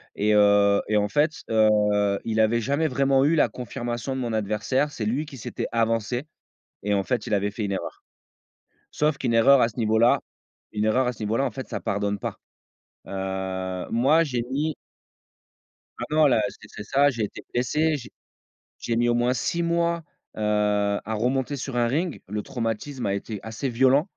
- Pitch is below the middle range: Yes, low, 120 Hz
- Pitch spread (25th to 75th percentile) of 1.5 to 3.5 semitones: No, average, 4.5 semitones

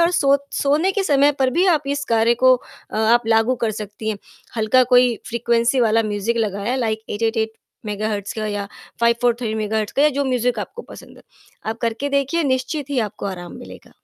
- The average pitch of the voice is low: No, high, 235 Hz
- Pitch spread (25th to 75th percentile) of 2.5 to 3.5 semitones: No, average, 3.9 semitones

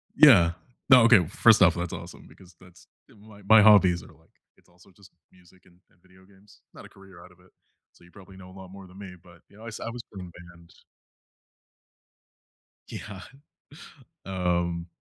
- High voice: No, very low, 95 Hz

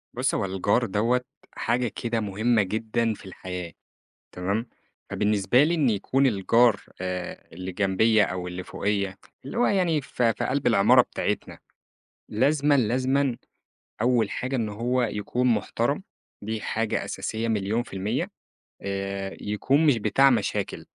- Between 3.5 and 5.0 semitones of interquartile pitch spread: Yes, average, 4.2 semitones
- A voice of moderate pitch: No, low, 110 Hz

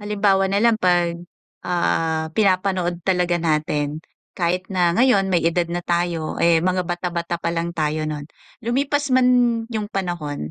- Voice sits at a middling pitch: Yes, medium, 175 Hz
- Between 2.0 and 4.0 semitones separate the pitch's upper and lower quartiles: Yes, average, 2.7 semitones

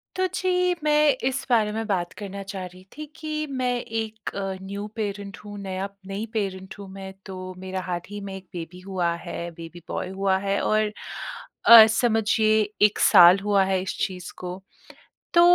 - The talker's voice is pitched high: Yes, high, 200 Hz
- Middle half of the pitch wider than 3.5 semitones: No, average, 2.9 semitones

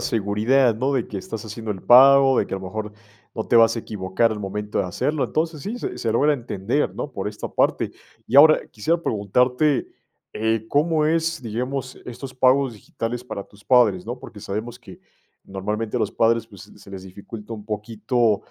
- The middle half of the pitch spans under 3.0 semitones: No, average, 4.1 semitones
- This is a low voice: Yes, low, 115 Hz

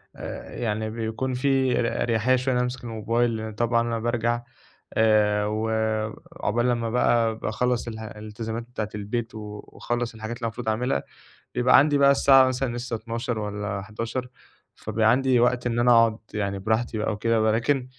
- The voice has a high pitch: No, low, 115 Hz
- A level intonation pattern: Yes, narrow, 2.0 semitones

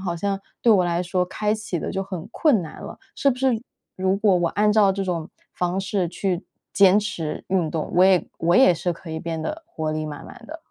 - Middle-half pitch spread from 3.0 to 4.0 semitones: Yes, average, 3.4 semitones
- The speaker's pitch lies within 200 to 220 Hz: No, medium, 185 Hz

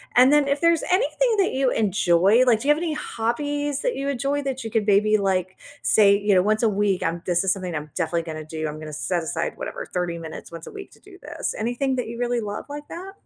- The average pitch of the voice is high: Yes, high, 220 Hz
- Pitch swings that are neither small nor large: No, wide, 7.5 semitones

